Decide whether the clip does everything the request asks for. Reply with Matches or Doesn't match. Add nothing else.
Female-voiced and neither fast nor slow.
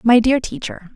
Matches